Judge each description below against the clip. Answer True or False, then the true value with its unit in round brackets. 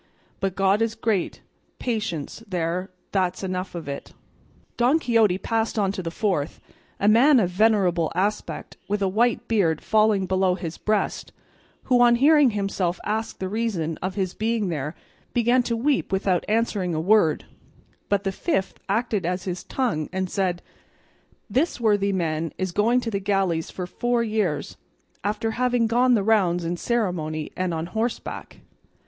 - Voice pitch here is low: False (200 Hz)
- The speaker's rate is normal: True (160 wpm)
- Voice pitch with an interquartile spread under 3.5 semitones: False (4.0 semitones)